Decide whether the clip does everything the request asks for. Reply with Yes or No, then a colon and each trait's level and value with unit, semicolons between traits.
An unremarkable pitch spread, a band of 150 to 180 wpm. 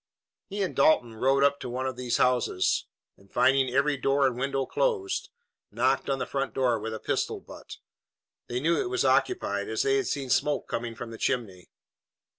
No: average, 3.1 semitones; average, 195 wpm